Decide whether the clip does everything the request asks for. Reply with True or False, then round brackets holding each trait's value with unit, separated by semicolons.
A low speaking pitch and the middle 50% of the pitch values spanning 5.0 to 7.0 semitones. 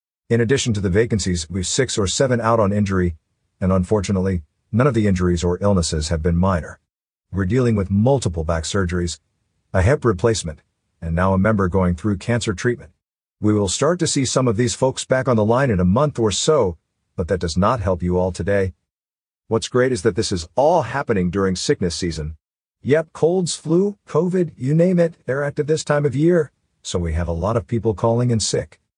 True (105 Hz; 5.4 semitones)